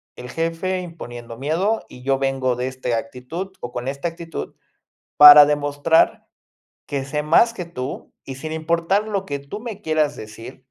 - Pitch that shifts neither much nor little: Yes, average, 4.3 semitones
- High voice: No, medium, 150 Hz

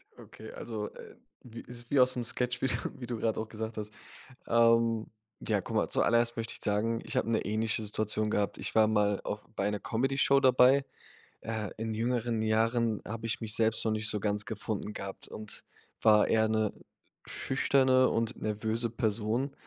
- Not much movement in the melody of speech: Yes, narrow, 1.7 semitones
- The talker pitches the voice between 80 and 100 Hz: No, low, 110 Hz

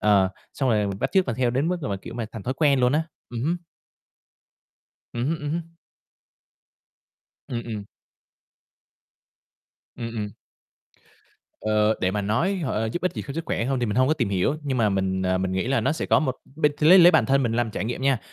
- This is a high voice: No, low, 120 Hz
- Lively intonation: Yes, wide, 5.7 semitones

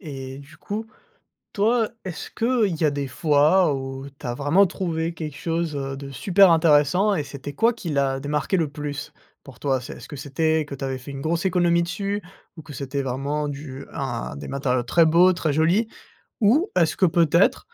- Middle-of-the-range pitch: Yes, medium, 150 Hz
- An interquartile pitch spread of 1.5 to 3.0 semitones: No, average, 4.2 semitones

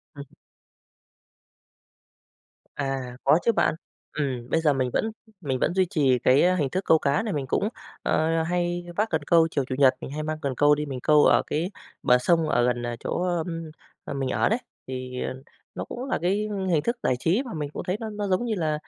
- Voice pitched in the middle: Yes, medium, 155 Hz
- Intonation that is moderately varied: Yes, average, 4.8 semitones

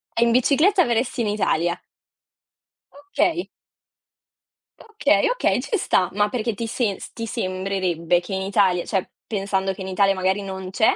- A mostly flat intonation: No, average, 3.8 semitones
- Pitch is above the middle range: Yes, high, 200 Hz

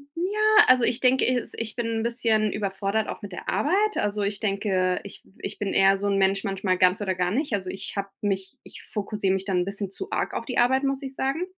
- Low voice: No, high, 205 Hz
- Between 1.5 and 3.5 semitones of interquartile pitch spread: No, average, 4.4 semitones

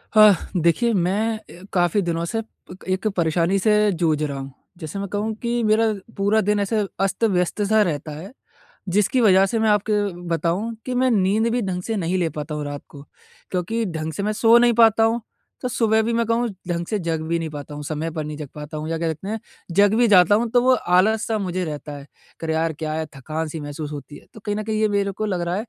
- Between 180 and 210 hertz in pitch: Yes, high, 190 Hz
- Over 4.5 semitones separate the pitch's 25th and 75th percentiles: Yes, average, 5.3 semitones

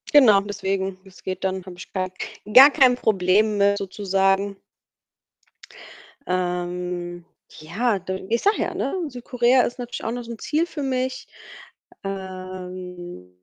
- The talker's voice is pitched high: Yes, high, 195 Hz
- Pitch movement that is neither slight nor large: Yes, average, 4.5 semitones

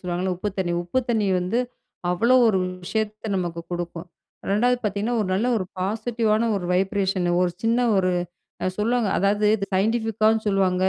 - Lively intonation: No, average, 3.3 semitones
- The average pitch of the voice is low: No, high, 205 Hz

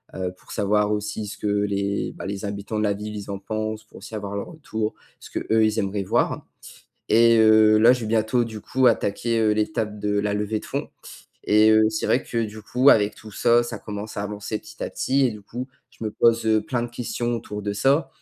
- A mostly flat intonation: Yes, narrow, 1.8 semitones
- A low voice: Yes, low, 110 Hz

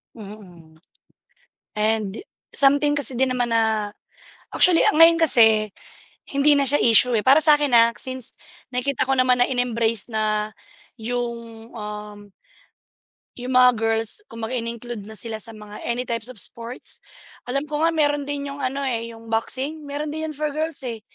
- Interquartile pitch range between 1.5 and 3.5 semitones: No, average, 4.0 semitones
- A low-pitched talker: No, high, 240 Hz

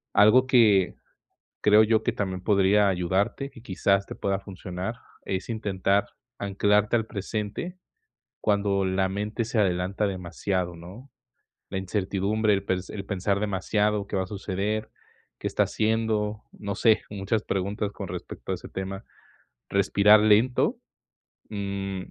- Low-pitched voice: Yes, low, 100 Hz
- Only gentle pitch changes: Yes, narrow, 1.9 semitones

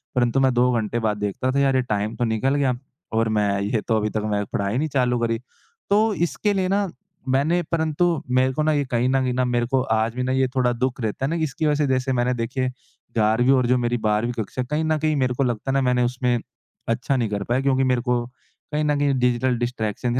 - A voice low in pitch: Yes, low, 125 Hz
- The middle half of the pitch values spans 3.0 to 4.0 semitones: No, narrow, 2.6 semitones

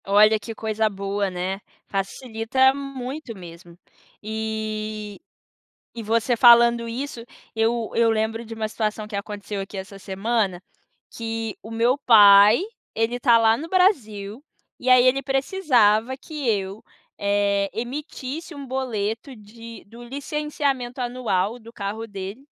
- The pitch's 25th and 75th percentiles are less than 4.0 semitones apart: Yes, average, 3.3 semitones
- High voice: Yes, high, 225 Hz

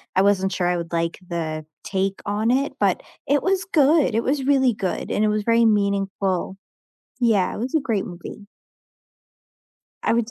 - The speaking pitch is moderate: No, high, 210 Hz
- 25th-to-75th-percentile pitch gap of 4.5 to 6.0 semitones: Yes, average, 5.2 semitones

